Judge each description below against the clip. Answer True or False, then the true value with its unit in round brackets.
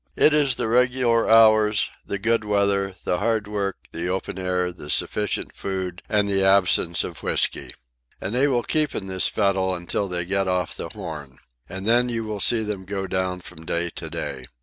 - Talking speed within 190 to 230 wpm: True (195 wpm)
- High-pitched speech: False (100 Hz)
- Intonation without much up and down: False (3.3 semitones)